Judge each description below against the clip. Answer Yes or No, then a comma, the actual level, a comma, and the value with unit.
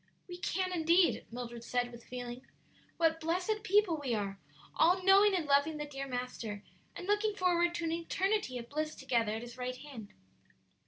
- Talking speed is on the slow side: No, average, 175 wpm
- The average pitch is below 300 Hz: No, very high, 310 Hz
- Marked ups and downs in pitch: Yes, wide, 6.6 semitones